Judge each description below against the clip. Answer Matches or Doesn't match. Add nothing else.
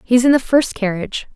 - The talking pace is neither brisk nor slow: Doesn't match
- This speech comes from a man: Doesn't match